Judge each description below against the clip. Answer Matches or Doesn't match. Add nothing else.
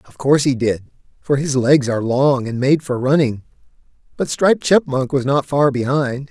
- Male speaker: Matches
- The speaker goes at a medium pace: Matches